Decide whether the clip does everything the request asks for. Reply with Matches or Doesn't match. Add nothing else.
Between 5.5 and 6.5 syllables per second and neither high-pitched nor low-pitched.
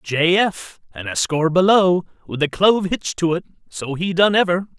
Doesn't match